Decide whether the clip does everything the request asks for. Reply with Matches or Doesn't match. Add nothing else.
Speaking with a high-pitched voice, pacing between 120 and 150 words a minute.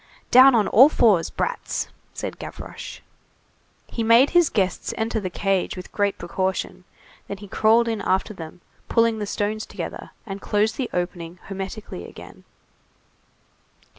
Matches